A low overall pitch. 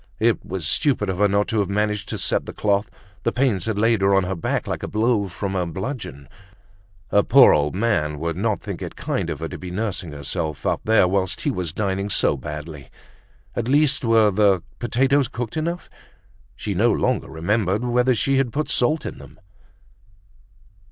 Yes: low, 105 Hz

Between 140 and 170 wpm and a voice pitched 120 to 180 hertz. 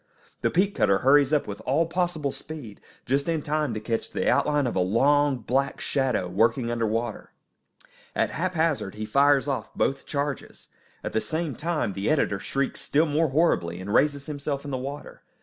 No: average, 185 wpm; medium, 140 Hz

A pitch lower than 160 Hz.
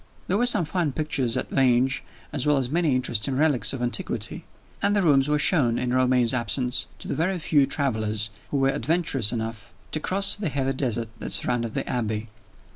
Yes: low, 135 Hz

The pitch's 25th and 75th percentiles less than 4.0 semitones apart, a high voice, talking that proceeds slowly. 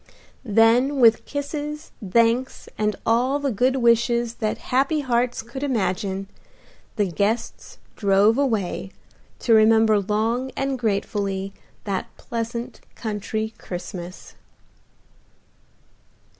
Yes: average, 3.6 semitones; high, 225 Hz; slow, 100 wpm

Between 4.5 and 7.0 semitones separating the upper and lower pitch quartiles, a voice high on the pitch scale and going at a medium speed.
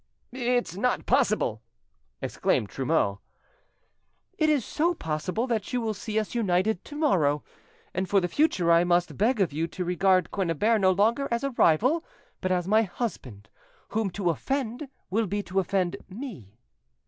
Yes: wide, 5.4 semitones; high, 200 Hz; average, 160 wpm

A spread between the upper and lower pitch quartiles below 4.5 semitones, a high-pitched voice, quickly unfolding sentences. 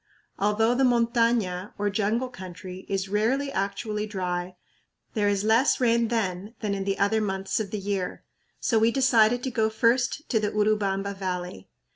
No: average, 3.0 semitones; high, 210 Hz; average, 165 wpm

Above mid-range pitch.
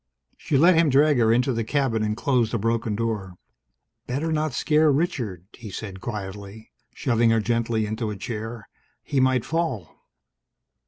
No: low, 115 Hz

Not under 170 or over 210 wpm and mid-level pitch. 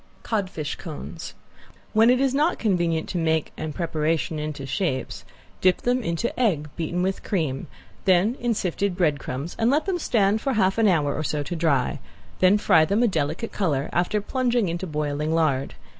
Yes: average, 175 wpm; medium, 175 Hz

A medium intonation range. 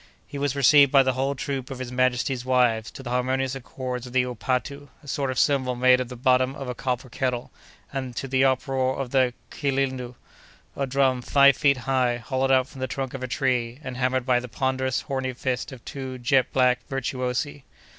No: narrow, 1.2 semitones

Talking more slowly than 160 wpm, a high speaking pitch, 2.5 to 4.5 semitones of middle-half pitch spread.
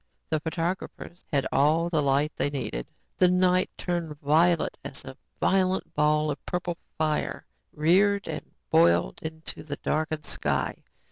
No: average, 140 wpm; medium, 160 Hz; average, 2.9 semitones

